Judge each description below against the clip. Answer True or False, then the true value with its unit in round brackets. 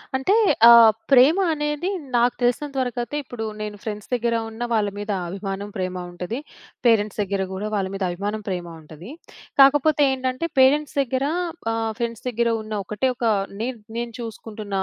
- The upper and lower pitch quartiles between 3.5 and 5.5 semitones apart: True (3.9 semitones)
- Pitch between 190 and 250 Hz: True (230 Hz)